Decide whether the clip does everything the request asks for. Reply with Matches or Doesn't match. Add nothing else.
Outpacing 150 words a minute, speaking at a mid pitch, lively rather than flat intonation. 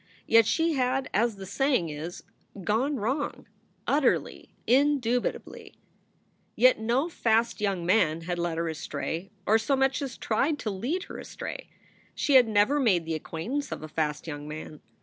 Doesn't match